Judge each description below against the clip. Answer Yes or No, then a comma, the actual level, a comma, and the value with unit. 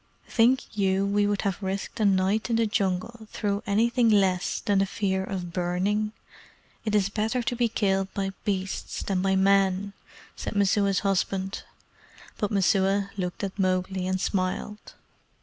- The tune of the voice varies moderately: No, narrow, 1.7 semitones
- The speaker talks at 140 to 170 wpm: Yes, average, 155 wpm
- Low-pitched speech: No, high, 195 Hz